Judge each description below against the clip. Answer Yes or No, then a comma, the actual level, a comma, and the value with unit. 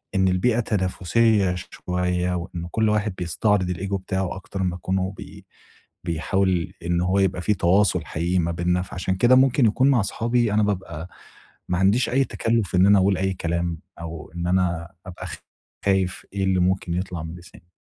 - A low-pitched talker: Yes, very low, 95 Hz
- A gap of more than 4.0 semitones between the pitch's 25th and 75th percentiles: No, narrow, 2.5 semitones